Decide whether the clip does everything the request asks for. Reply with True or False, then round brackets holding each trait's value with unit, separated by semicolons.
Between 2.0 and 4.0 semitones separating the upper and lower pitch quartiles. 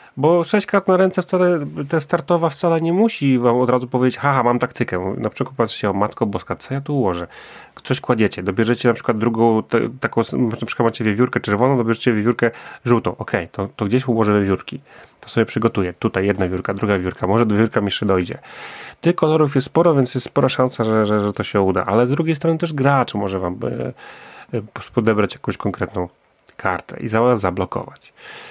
False (4.8 semitones)